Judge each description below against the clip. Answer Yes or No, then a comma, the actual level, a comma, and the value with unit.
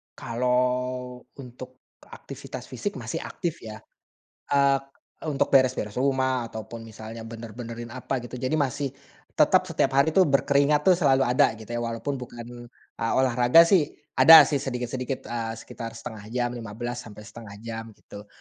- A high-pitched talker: No, low, 125 Hz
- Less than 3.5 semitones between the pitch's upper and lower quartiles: Yes, narrow, 2.6 semitones